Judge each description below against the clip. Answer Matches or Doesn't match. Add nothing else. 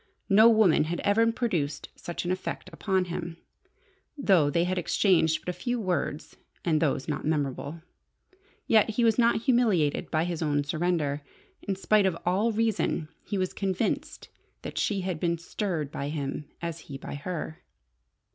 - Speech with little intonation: Doesn't match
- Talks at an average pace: Matches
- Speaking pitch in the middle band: Matches